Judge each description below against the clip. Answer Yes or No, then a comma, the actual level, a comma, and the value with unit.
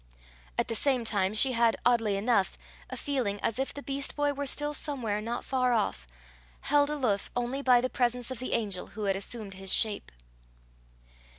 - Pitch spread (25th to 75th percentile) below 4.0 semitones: No, average, 4.3 semitones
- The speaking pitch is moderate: No, high, 240 Hz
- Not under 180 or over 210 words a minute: Yes, average, 185 wpm